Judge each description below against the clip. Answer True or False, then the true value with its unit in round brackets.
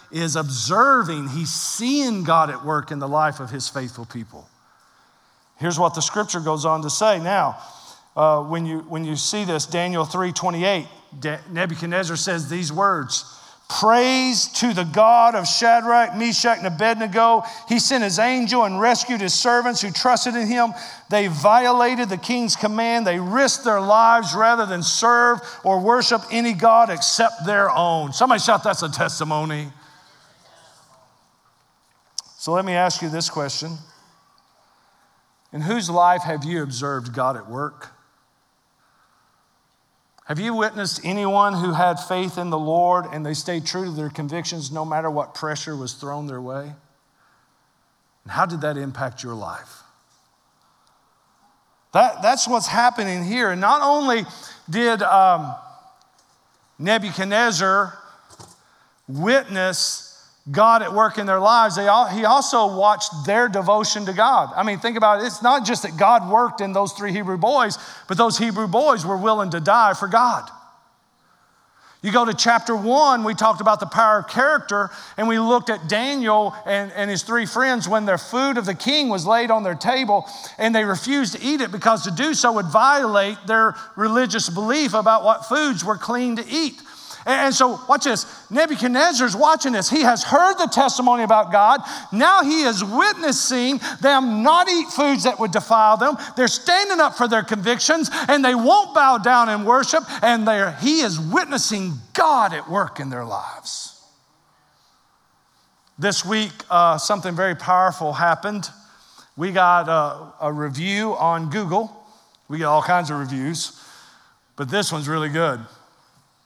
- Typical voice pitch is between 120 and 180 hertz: False (210 Hz)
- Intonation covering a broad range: True (5.7 semitones)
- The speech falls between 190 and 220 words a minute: False (160 wpm)